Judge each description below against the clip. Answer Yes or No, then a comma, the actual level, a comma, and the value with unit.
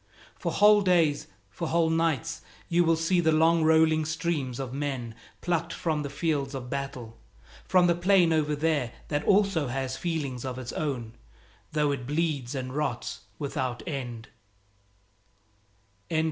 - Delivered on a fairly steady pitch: No, average, 3.8 semitones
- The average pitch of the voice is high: No, medium, 150 Hz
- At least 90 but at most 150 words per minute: Yes, average, 145 wpm